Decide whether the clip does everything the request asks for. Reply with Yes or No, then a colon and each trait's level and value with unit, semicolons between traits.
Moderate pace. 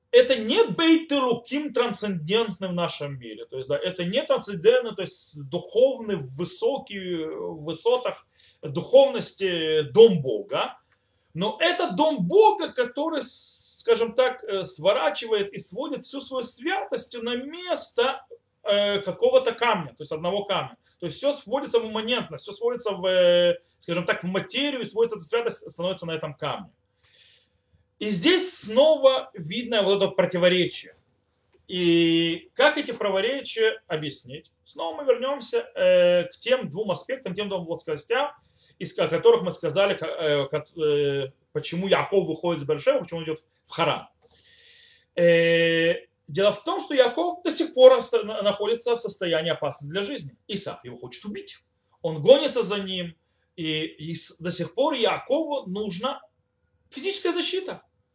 Yes: average, 140 wpm